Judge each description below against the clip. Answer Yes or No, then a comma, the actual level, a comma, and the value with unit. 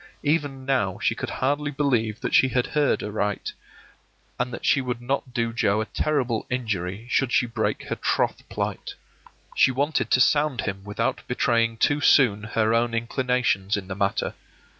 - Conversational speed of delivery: Yes, average, 170 wpm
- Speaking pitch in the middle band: No, low, 120 Hz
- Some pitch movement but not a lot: Yes, average, 3.6 semitones